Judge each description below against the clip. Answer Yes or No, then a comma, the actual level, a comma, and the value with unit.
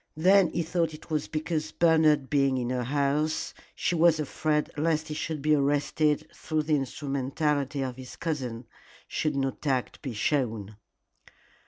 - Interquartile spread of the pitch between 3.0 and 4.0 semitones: No, narrow, 2.6 semitones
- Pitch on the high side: No, medium, 150 Hz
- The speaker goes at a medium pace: Yes, average, 155 wpm